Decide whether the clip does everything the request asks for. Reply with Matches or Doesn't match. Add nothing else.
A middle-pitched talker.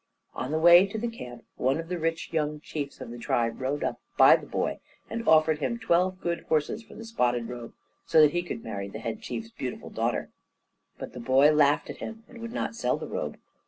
Matches